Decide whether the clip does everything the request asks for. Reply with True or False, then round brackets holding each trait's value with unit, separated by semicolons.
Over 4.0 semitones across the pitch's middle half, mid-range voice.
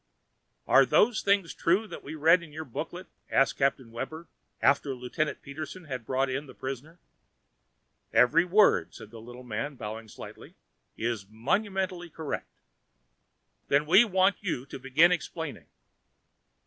True (5.6 semitones; 150 Hz)